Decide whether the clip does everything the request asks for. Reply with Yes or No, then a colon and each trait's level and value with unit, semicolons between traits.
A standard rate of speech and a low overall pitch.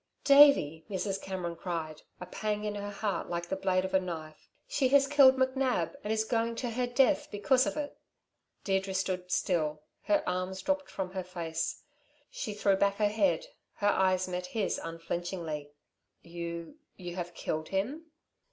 No: average, 170 wpm; high, 190 Hz